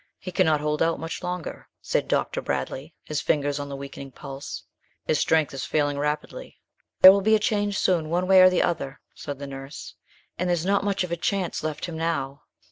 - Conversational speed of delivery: No, fast, 210 wpm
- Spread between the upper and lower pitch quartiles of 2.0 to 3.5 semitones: No, average, 4.2 semitones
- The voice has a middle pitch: Yes, medium, 160 Hz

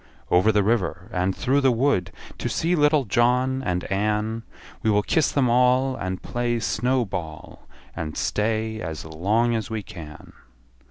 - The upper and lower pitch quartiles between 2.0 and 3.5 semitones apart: No, average, 5.1 semitones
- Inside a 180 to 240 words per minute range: No, average, 160 wpm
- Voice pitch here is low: Yes, low, 110 Hz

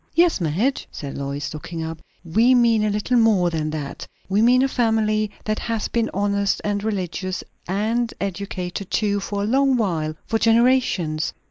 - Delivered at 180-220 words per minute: No, average, 165 wpm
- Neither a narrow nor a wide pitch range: Yes, average, 4.6 semitones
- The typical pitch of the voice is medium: No, high, 205 Hz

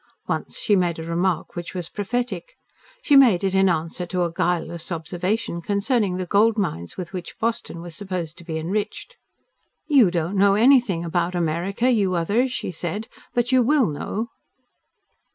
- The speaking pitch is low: No, medium, 185 Hz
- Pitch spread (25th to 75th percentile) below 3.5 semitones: No, average, 4.5 semitones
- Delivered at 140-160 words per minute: No, average, 170 wpm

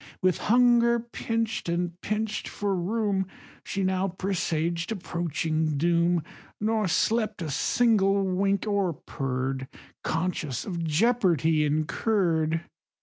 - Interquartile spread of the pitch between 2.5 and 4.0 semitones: No, average, 4.6 semitones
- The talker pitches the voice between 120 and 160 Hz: No, medium, 185 Hz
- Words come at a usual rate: No, slow, 105 wpm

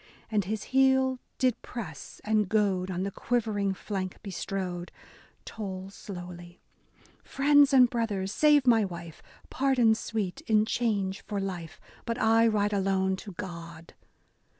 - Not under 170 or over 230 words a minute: No, average, 150 wpm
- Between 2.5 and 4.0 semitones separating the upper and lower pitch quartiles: Yes, average, 3.6 semitones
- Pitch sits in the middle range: No, high, 205 Hz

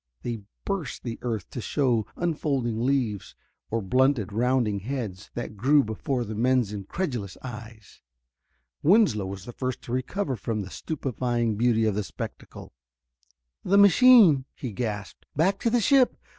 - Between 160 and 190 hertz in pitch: No, low, 120 Hz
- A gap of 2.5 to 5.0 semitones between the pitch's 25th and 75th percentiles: Yes, average, 4.6 semitones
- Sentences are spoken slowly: No, average, 145 wpm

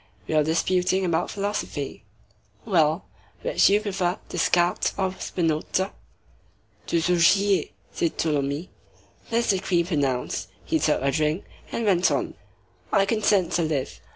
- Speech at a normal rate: No, slow, 125 wpm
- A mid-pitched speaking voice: Yes, medium, 175 Hz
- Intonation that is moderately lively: Yes, average, 3.7 semitones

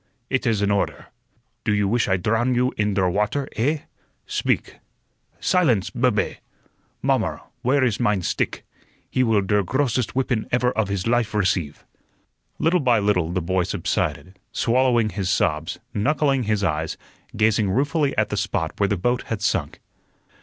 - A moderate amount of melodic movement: Yes, average, 4.4 semitones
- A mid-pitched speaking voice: No, low, 110 Hz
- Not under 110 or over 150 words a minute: No, average, 160 wpm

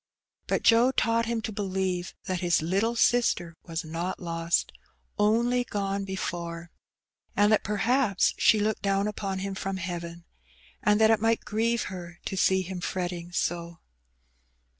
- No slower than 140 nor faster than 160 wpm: Yes, average, 155 wpm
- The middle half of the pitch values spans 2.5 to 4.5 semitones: Yes, average, 3.8 semitones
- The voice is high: Yes, high, 195 Hz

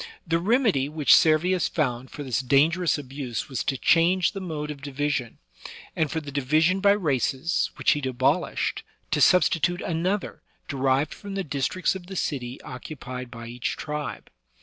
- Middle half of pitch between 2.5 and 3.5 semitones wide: No, average, 4.8 semitones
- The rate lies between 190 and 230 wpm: No, average, 165 wpm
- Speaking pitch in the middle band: Yes, medium, 150 Hz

